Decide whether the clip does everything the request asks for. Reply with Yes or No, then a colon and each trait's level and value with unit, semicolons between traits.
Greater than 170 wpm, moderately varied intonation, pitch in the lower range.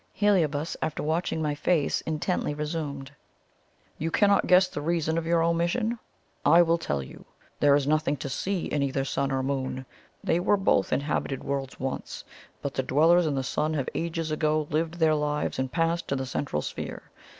No: average, 185 wpm; average, 3.2 semitones; medium, 155 Hz